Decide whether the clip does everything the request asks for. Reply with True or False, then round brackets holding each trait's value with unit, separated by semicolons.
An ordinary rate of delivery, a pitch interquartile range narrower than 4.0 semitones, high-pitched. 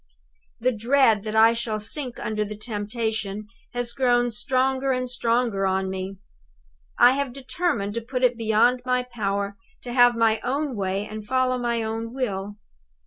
True (160 wpm; 3.0 semitones; 230 Hz)